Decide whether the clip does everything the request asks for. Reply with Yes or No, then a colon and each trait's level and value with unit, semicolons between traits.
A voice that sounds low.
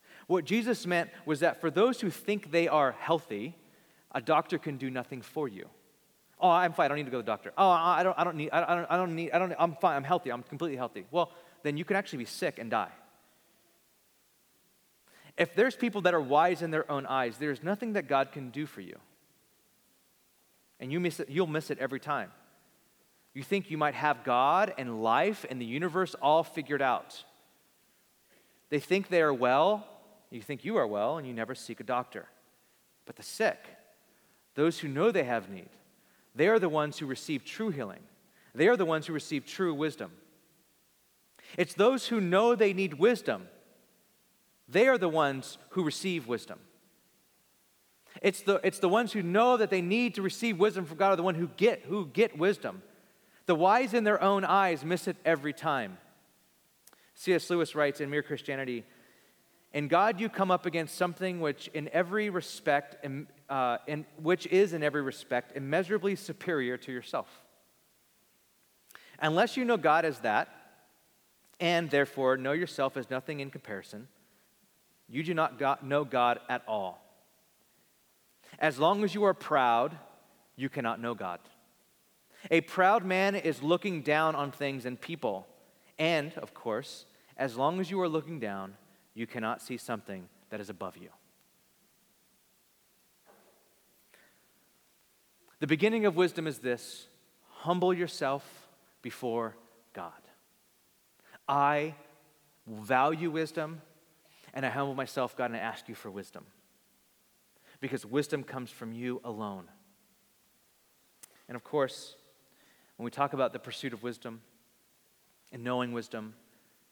No: medium, 155 Hz